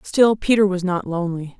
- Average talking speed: Yes, average, 190 wpm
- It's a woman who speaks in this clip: Yes, female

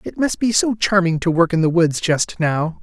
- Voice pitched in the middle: Yes, medium, 180 Hz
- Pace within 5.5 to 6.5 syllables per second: No, 4.8 syllables/s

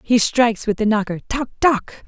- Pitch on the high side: Yes, high, 230 Hz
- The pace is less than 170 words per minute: No, average, 200 wpm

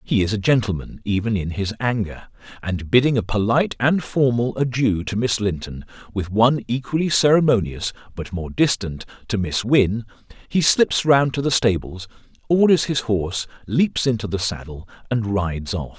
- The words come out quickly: No, average, 165 wpm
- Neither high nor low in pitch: No, low, 110 Hz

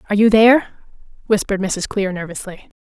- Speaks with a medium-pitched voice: No, high, 200 Hz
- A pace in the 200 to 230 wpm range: No, average, 150 wpm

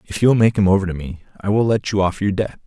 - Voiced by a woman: No, male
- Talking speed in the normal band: No, fast, 340 wpm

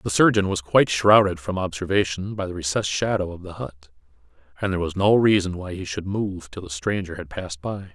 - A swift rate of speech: Yes, fast, 220 wpm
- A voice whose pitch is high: No, very low, 90 Hz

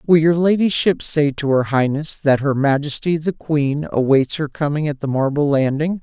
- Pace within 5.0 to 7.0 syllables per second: No, 4.8 syllables/s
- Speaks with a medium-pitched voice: Yes, medium, 145 Hz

